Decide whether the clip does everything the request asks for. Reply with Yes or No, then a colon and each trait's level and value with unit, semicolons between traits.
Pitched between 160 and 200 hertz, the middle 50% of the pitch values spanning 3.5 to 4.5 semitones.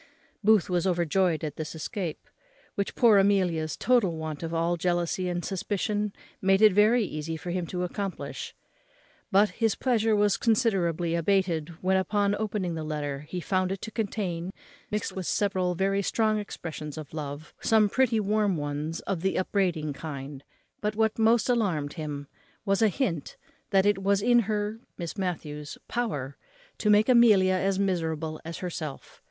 Yes: medium, 185 Hz; average, 4.2 semitones